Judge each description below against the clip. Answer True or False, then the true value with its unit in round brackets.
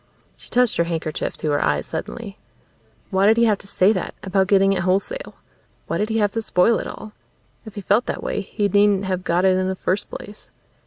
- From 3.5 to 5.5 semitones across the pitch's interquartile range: False (2.4 semitones)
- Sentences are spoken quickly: True (225 wpm)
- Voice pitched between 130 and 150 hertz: False (195 Hz)